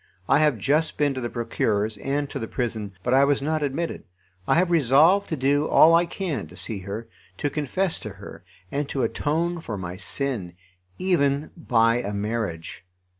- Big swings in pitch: Yes, wide, 5.7 semitones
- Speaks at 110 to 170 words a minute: No, average, 185 wpm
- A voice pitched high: No, low, 135 Hz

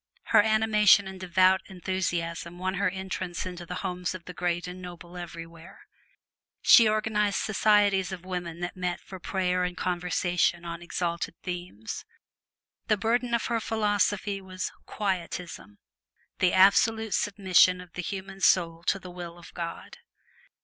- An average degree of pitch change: No, narrow, 2.1 semitones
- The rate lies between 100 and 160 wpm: Yes, average, 145 wpm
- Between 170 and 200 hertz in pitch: Yes, medium, 185 Hz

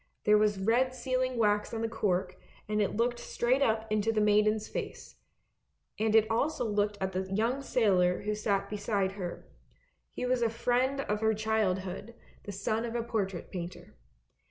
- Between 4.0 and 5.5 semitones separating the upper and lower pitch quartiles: No, narrow, 2.5 semitones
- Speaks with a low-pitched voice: No, high, 215 Hz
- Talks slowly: No, average, 175 wpm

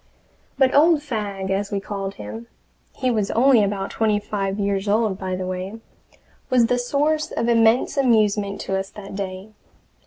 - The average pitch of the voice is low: No, high, 210 Hz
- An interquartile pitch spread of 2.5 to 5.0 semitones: Yes, average, 3.4 semitones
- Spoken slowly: No, average, 165 wpm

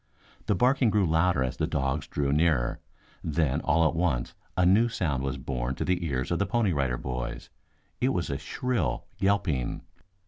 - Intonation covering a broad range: Yes, wide, 5.7 semitones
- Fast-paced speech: No, average, 180 wpm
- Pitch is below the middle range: Yes, very low, 80 Hz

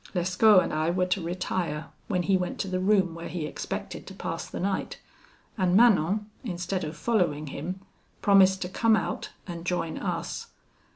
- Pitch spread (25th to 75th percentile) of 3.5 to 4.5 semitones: No, narrow, 2.4 semitones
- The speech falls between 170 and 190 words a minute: Yes, average, 175 wpm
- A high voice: No, medium, 180 Hz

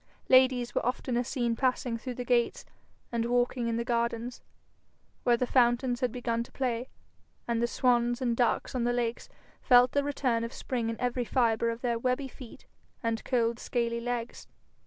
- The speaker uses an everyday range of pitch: No, narrow, 1.3 semitones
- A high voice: Yes, high, 240 Hz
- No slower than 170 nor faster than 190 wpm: Yes, average, 180 wpm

